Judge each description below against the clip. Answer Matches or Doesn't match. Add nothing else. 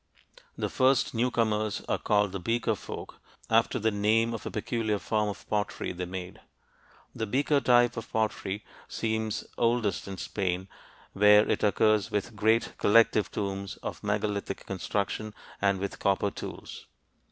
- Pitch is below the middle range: Matches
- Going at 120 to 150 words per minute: Matches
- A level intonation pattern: Matches